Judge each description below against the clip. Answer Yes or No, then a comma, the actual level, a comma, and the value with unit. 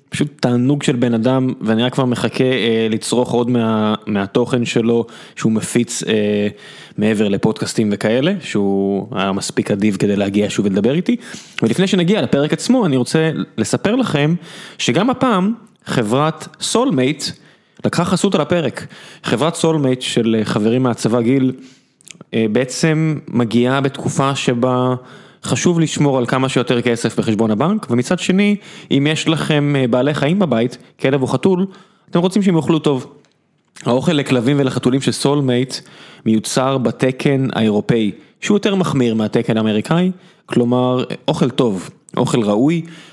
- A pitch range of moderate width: No, wide, 5.8 semitones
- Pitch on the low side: Yes, low, 130 Hz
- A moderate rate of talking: Yes, average, 140 wpm